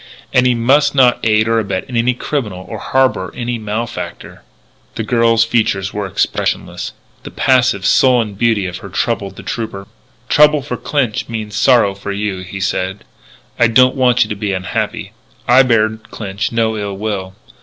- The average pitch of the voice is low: Yes, low, 110 Hz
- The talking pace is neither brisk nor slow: Yes, average, 165 wpm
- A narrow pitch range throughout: No, average, 3.5 semitones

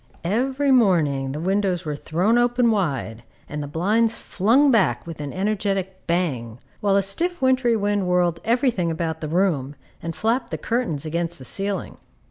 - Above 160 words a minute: Yes, average, 170 wpm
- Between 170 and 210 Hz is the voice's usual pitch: Yes, high, 190 Hz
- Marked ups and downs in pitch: Yes, wide, 5.9 semitones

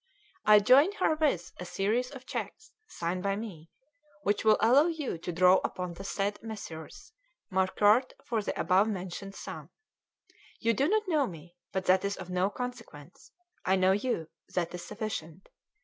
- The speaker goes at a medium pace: Yes, average, 165 wpm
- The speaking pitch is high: Yes, high, 200 Hz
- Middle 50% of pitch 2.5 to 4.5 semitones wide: No, average, 5.2 semitones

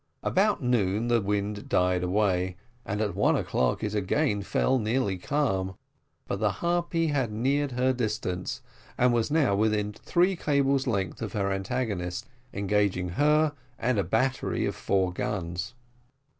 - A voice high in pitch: No, low, 105 Hz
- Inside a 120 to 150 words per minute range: Yes, average, 145 wpm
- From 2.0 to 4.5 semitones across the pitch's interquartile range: No, wide, 5.4 semitones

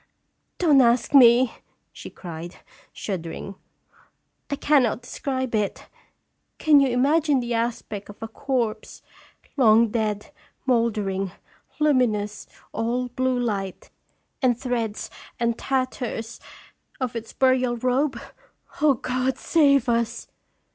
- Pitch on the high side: Yes, high, 240 Hz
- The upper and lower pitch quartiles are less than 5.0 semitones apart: Yes, average, 2.9 semitones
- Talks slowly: Yes, slow, 115 wpm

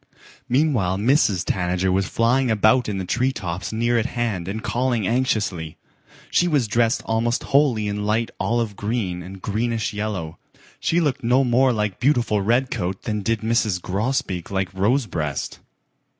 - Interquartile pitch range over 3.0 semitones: Yes, average, 4.0 semitones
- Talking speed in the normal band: Yes, average, 150 wpm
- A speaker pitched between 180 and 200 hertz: No, low, 110 Hz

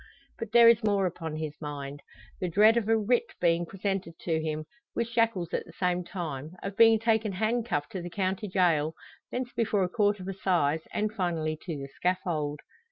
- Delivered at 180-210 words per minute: Yes, average, 190 wpm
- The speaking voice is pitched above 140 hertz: Yes, medium, 185 Hz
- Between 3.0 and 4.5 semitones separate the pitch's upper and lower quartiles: No, average, 5.0 semitones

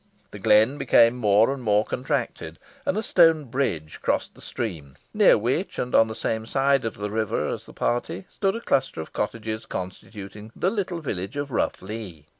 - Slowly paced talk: No, average, 190 wpm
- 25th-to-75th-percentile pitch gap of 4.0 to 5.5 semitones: Yes, average, 5.1 semitones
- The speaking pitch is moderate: No, low, 115 Hz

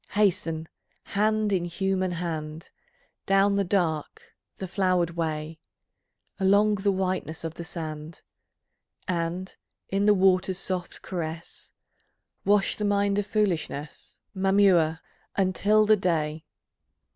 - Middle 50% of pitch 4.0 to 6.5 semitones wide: No, average, 3.4 semitones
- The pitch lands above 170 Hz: Yes, medium, 185 Hz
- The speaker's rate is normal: No, slow, 110 wpm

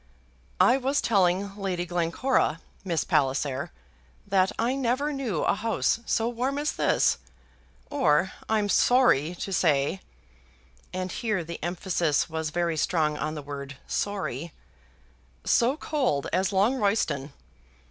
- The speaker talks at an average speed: No, slow, 125 wpm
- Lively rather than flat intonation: Yes, wide, 6.4 semitones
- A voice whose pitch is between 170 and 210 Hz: Yes, high, 190 Hz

